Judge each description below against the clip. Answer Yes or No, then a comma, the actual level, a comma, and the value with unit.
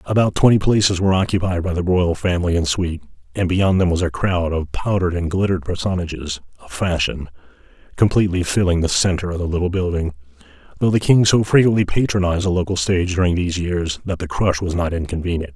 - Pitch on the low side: Yes, very low, 90 Hz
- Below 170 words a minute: No, average, 195 wpm